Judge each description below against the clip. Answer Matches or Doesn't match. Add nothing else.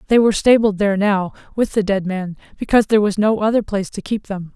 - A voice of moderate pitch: Doesn't match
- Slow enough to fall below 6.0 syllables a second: Doesn't match